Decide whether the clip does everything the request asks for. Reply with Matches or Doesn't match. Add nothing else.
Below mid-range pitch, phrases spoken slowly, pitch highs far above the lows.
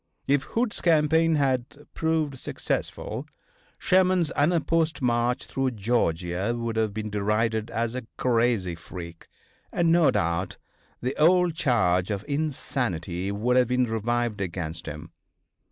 Matches